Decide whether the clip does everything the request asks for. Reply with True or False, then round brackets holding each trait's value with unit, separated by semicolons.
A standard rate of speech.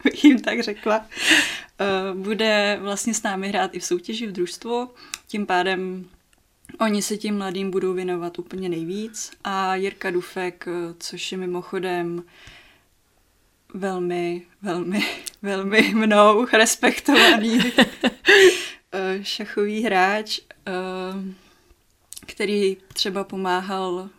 False (100 wpm)